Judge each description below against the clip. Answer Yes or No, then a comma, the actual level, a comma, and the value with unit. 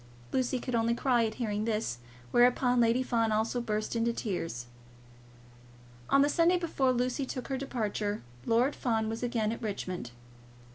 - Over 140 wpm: Yes, average, 155 wpm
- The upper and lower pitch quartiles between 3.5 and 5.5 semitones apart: No, average, 2.8 semitones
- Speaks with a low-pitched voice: No, high, 235 Hz